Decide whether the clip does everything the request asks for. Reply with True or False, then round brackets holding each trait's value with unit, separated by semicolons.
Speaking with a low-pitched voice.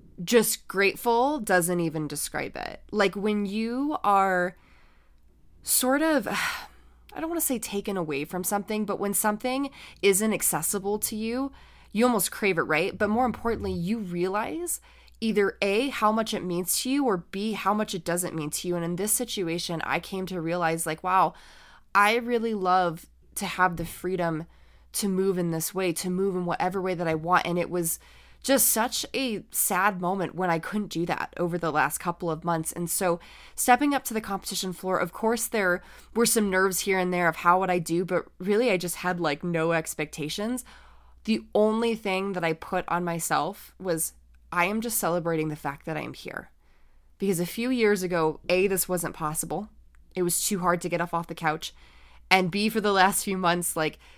False (185 Hz)